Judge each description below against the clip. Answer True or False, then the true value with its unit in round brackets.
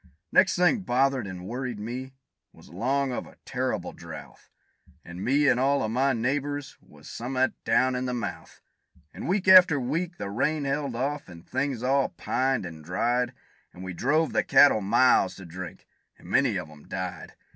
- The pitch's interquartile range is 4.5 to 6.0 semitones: True (5.3 semitones)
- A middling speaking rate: True (180 wpm)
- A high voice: False (130 Hz)